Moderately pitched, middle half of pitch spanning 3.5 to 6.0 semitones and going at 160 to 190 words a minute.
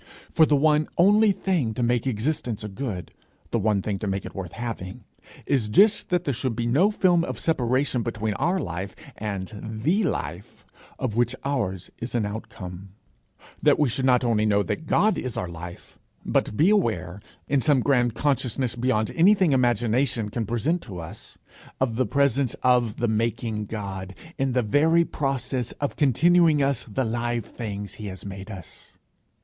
No: low, 120 Hz; average, 5.0 semitones; average, 175 wpm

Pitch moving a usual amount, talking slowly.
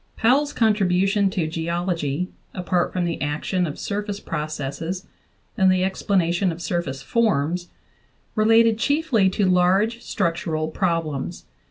Yes: average, 3.7 semitones; slow, 125 wpm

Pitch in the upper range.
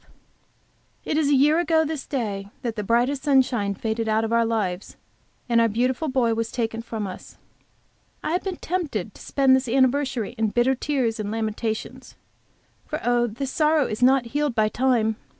Yes: high, 240 Hz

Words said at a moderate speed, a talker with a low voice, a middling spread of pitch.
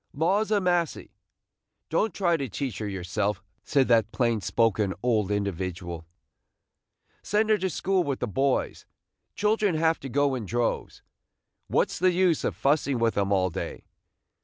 No: average, 160 wpm; low, 130 Hz; wide, 8.9 semitones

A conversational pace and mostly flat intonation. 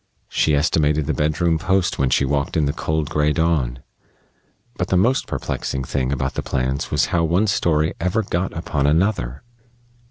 No: average, 170 wpm; average, 3.7 semitones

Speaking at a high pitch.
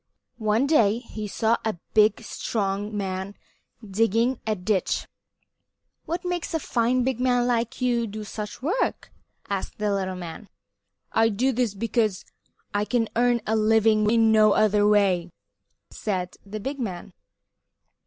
Yes: high, 220 Hz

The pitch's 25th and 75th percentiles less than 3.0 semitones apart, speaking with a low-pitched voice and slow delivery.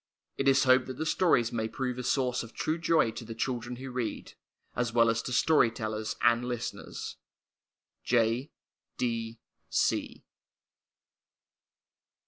Yes: narrow, 2.5 semitones; low, 125 Hz; slow, 130 wpm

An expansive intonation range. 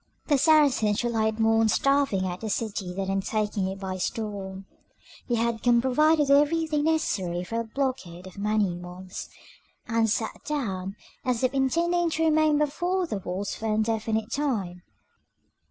Yes: wide, 6.4 semitones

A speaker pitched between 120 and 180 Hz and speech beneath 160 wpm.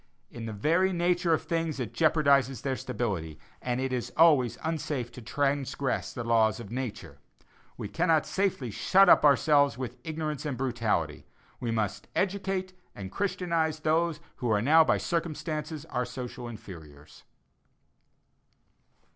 Yes: medium, 140 Hz; average, 140 wpm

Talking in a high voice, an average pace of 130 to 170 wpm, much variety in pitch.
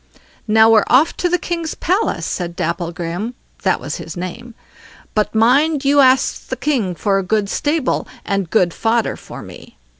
Yes: high, 225 Hz; average, 160 wpm; wide, 6.8 semitones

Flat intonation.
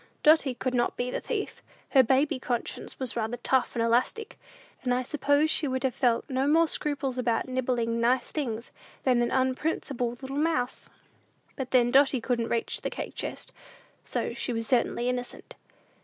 Yes: narrow, 2.3 semitones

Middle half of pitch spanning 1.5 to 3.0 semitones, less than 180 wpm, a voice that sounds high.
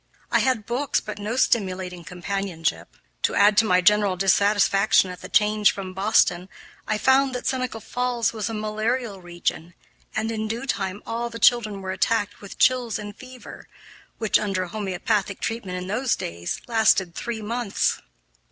No: average, 3.4 semitones; average, 160 wpm; high, 210 Hz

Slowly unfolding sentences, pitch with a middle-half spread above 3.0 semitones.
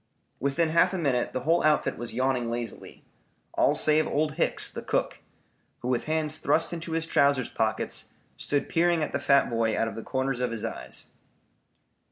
No: average, 185 wpm; average, 4.7 semitones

